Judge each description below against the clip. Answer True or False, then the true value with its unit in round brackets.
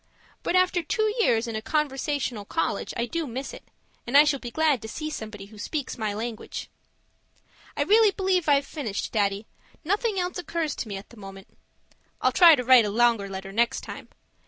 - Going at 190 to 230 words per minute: True (195 wpm)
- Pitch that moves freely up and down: True (6.8 semitones)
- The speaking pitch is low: False (255 Hz)